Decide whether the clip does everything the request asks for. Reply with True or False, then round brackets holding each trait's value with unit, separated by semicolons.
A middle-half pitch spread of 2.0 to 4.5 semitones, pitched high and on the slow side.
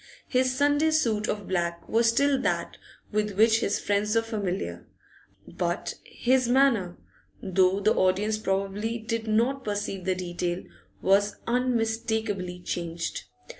True (3.5 semitones; 215 Hz; 130 wpm)